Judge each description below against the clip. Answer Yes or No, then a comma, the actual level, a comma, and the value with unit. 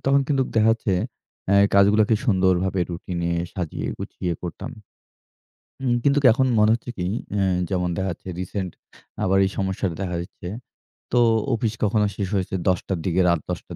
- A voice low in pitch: Yes, very low, 95 Hz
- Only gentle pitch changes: No, average, 3.2 semitones